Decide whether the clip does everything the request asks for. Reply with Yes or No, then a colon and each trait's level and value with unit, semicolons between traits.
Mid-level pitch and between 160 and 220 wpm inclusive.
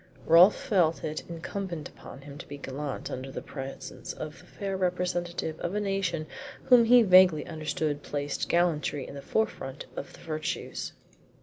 Yes: medium, 165 Hz; average, 165 wpm